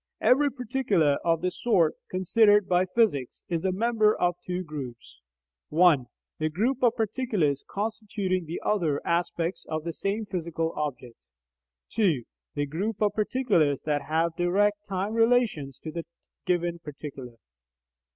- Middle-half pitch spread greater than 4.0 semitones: Yes, average, 5.3 semitones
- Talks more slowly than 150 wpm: Yes, average, 140 wpm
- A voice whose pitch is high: No, medium, 180 Hz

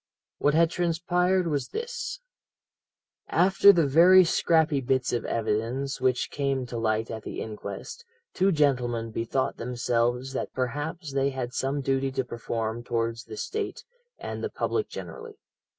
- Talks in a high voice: No, low, 135 Hz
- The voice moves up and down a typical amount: No, wide, 5.9 semitones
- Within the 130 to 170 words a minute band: Yes, average, 145 wpm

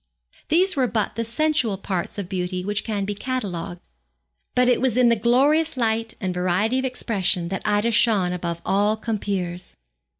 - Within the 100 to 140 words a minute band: No, average, 170 wpm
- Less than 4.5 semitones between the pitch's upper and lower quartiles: No, average, 4.9 semitones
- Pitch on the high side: Yes, high, 210 Hz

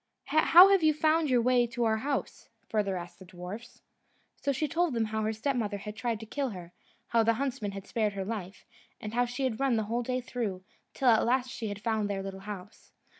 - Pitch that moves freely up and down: No, average, 3.8 semitones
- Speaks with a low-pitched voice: No, high, 230 Hz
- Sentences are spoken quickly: Yes, fast, 225 wpm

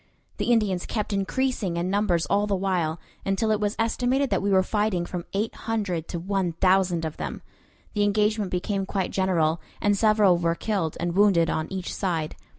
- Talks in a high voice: Yes, high, 195 Hz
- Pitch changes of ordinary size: Yes, average, 3.2 semitones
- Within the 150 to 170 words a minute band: No, average, 185 wpm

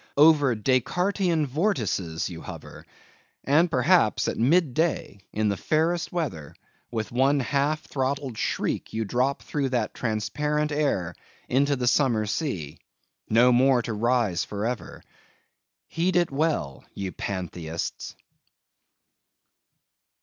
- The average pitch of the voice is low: Yes, low, 130 Hz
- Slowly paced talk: Yes, slow, 120 wpm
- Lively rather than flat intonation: Yes, wide, 6.0 semitones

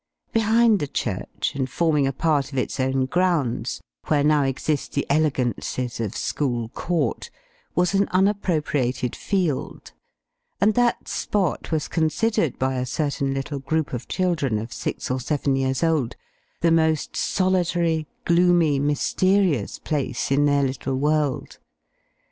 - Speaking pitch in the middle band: Yes, medium, 150 Hz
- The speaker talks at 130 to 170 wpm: Yes, slow, 135 wpm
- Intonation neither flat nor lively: Yes, average, 4.6 semitones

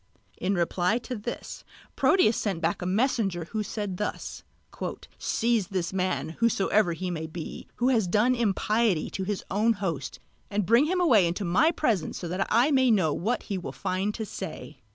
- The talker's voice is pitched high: Yes, high, 205 Hz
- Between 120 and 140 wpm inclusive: No, average, 175 wpm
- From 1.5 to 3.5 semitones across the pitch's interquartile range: No, average, 4.3 semitones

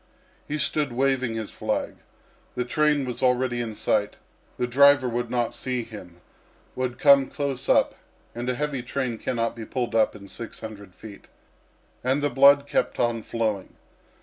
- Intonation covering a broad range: No, average, 3.2 semitones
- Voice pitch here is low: Yes, low, 125 Hz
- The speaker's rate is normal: Yes, average, 165 wpm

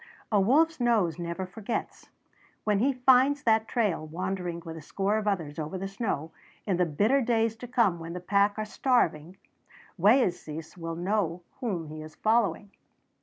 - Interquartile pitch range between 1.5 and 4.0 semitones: No, average, 5.1 semitones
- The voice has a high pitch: Yes, high, 195 Hz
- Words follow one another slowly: No, average, 170 wpm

